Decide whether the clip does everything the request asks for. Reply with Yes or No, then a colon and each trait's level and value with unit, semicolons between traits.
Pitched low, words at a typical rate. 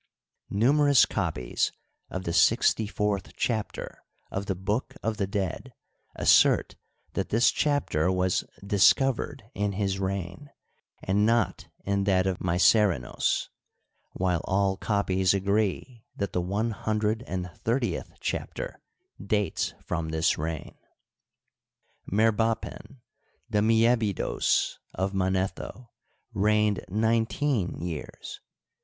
No: low, 100 Hz; slow, 110 wpm